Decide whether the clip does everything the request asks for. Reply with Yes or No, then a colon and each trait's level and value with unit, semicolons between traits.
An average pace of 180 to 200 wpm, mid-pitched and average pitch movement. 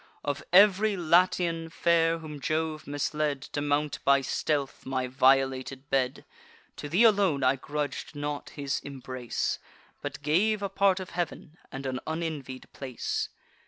No: average, 140 wpm; medium, 150 Hz; average, 3.8 semitones